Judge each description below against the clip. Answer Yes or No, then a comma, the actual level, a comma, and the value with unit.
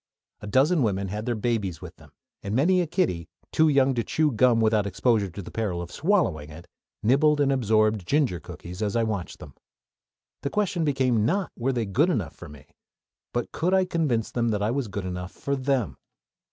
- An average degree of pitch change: No, wide, 5.8 semitones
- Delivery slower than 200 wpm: No, fast, 205 wpm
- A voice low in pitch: Yes, low, 115 Hz